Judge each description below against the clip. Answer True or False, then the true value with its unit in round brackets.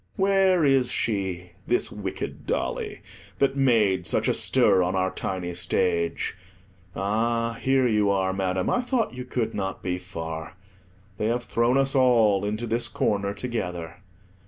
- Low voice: True (105 Hz)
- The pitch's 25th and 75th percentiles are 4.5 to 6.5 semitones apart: True (5.1 semitones)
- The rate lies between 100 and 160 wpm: True (150 wpm)